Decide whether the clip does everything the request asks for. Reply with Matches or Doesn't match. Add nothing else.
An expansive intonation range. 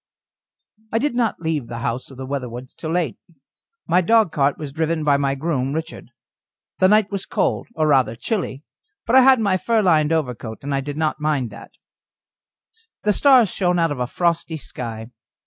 Matches